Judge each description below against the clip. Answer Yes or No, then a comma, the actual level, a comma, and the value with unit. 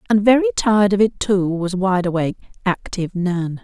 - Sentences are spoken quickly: No, average, 180 wpm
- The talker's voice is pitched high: Yes, high, 195 Hz